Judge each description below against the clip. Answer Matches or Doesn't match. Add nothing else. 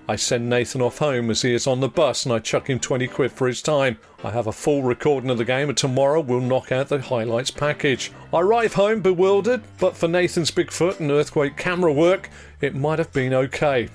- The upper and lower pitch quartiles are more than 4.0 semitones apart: Matches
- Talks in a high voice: Doesn't match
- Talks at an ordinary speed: Doesn't match